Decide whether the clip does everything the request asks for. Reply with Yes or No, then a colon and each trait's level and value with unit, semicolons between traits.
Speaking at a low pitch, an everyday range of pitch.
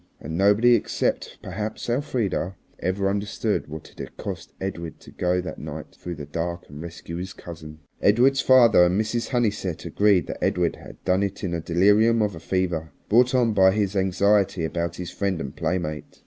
Yes: very low, 95 Hz; average, 3.7 semitones